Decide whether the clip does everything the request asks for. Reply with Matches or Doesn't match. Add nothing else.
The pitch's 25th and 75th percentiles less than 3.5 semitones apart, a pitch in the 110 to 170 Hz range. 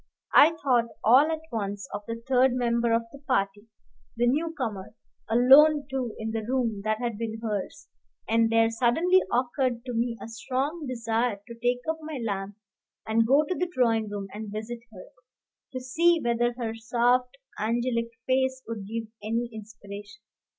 Doesn't match